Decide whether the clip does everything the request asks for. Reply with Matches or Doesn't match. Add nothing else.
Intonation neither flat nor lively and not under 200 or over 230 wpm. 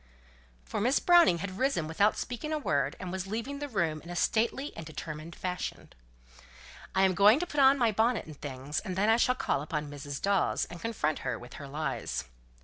Doesn't match